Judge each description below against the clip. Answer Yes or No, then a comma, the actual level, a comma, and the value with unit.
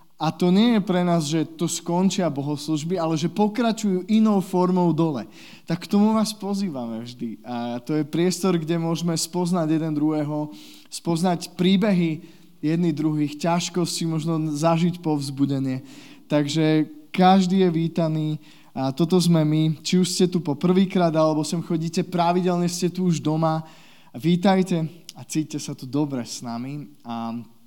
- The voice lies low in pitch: No, medium, 165 Hz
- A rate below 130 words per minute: No, average, 150 wpm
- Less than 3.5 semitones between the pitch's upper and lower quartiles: Yes, average, 2.9 semitones